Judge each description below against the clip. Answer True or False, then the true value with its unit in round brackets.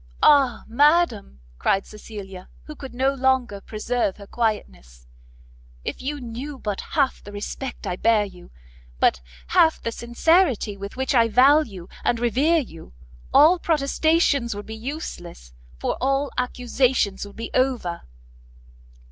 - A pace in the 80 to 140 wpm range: True (135 wpm)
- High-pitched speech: True (240 Hz)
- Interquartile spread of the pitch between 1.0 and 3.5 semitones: False (5.2 semitones)